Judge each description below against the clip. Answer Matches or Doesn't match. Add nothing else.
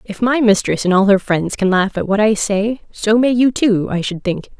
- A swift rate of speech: Matches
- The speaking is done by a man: Doesn't match